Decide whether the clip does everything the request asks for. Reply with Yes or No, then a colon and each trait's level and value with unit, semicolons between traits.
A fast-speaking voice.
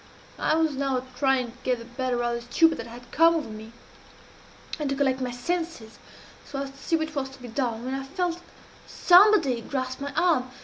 Yes: fast, 210 wpm